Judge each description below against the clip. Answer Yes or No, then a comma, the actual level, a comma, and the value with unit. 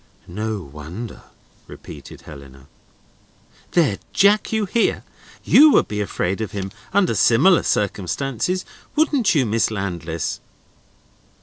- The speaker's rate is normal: No, slow, 110 wpm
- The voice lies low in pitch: Yes, low, 110 Hz